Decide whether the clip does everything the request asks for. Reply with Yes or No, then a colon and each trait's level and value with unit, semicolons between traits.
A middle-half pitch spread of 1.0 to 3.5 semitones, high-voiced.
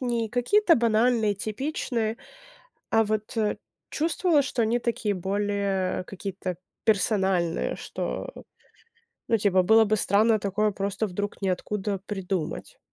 Yes: average, 2.7 semitones; high, 210 Hz